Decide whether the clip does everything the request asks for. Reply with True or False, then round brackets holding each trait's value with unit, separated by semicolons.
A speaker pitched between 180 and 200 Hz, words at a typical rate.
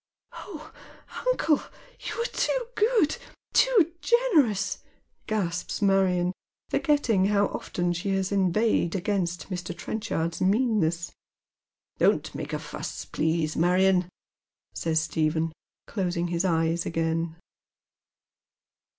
False (185 Hz; 105 wpm)